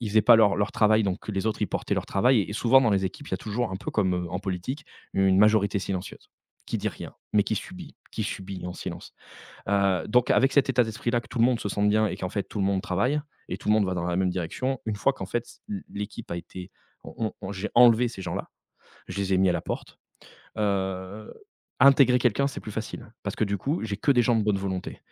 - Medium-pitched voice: No, low, 105 Hz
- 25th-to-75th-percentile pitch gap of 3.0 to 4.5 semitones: Yes, average, 3.7 semitones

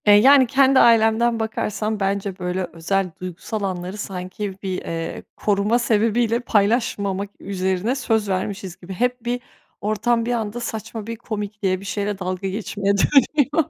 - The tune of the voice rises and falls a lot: No, average, 3.3 semitones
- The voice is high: Yes, high, 210 Hz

